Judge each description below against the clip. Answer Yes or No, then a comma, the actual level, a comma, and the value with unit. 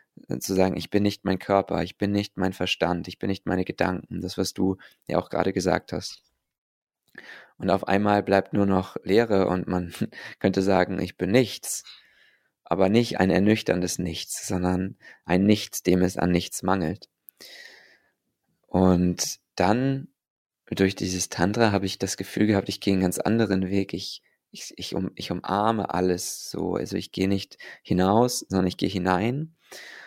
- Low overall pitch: Yes, very low, 95 Hz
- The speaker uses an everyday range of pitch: No, narrow, 1.9 semitones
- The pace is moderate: Yes, average, 170 wpm